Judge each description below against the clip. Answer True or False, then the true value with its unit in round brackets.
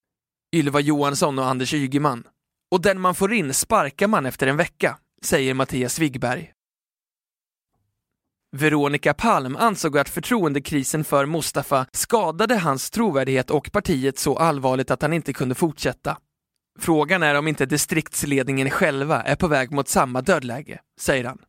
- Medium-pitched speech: True (145 Hz)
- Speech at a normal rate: True (140 wpm)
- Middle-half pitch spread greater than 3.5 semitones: True (4.3 semitones)